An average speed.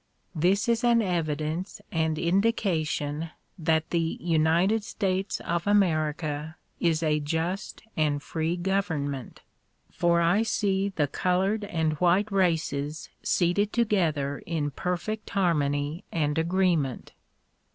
No: slow, 110 wpm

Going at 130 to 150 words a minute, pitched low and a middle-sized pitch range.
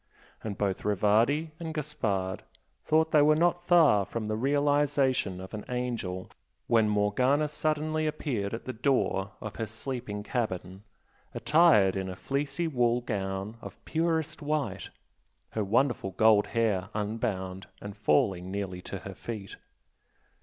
No: average, 140 wpm; low, 115 Hz; wide, 6.5 semitones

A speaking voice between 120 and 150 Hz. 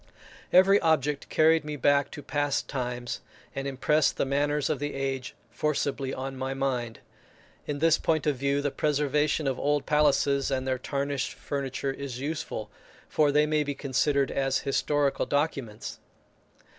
Yes: medium, 140 Hz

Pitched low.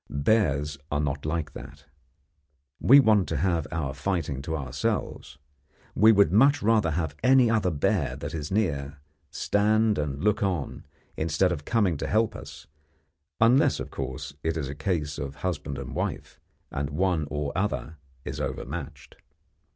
Yes: very low, 80 Hz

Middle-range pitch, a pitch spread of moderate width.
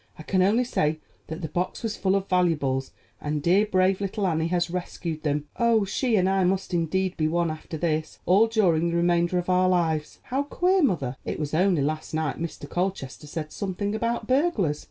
Yes: medium, 180 Hz; average, 3.8 semitones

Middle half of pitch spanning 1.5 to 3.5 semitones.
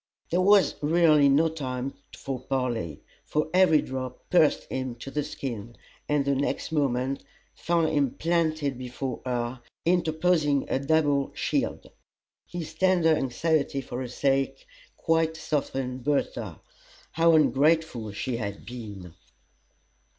No: average, 4.0 semitones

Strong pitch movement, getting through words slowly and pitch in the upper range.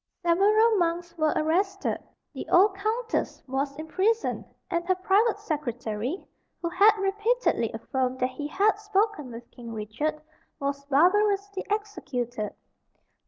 Yes: wide, 6.9 semitones; slow, 120 wpm; very high, 345 Hz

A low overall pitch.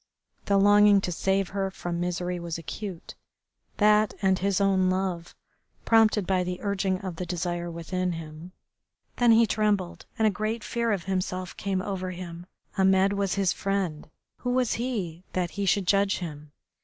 No: high, 190 Hz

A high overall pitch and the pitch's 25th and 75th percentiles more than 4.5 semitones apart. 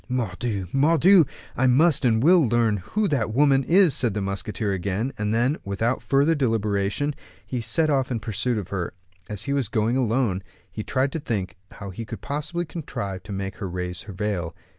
No: low, 115 Hz; wide, 5.6 semitones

